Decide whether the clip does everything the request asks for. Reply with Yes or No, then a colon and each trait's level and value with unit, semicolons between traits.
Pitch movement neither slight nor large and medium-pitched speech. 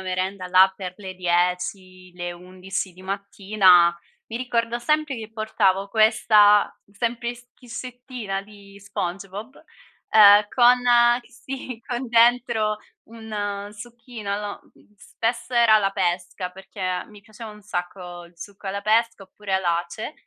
No: average, 3.5 semitones; high, 205 Hz